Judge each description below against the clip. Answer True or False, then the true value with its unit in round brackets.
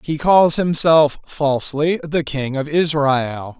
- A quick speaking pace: False (135 wpm)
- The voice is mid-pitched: True (150 Hz)